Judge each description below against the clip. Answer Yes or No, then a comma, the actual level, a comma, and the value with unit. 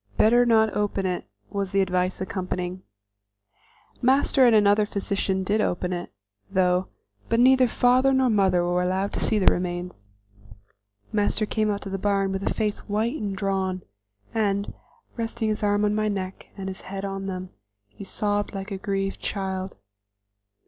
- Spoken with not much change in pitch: Yes, narrow, 2.3 semitones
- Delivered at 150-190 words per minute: Yes, average, 165 wpm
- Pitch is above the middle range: Yes, high, 195 Hz